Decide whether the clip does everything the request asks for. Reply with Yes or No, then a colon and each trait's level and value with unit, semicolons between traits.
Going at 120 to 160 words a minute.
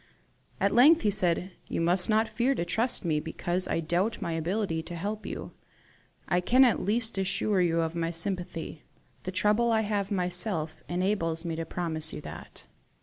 No: average, 185 wpm